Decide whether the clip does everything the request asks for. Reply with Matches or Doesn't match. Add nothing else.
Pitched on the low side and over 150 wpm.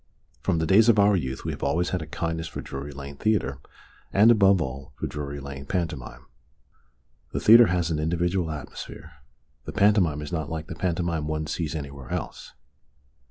Matches